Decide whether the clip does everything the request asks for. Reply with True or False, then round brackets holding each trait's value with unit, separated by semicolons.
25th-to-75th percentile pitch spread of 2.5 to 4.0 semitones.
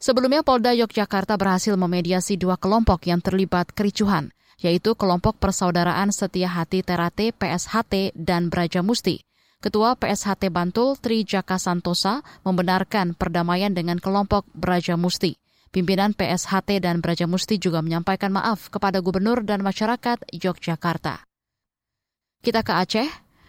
True (2.8 semitones)